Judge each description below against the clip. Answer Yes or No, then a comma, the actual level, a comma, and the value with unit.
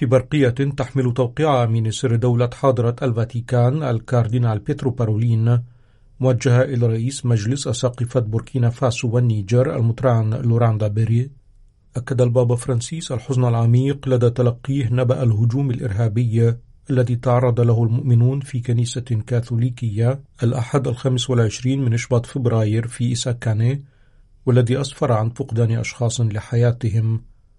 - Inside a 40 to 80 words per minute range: No, average, 115 wpm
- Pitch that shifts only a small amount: Yes, narrow, 1.8 semitones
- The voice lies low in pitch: Yes, low, 120 Hz